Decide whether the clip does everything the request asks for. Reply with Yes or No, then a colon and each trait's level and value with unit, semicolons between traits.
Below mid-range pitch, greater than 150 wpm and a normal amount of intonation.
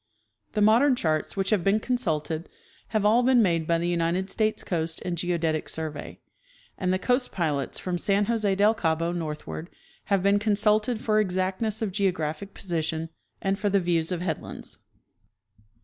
No: medium, 185 Hz; average, 165 wpm; average, 4.2 semitones